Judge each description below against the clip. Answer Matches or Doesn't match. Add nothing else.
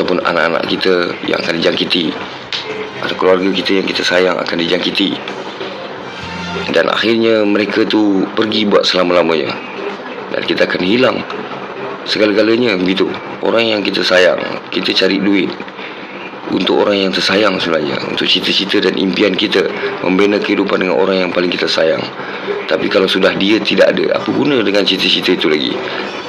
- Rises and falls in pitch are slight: Matches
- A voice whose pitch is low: Matches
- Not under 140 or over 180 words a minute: Matches